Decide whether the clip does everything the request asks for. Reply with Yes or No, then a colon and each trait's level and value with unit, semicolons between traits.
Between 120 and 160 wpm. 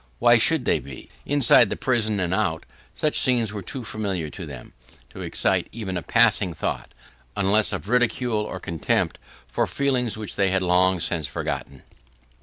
No: average, 170 wpm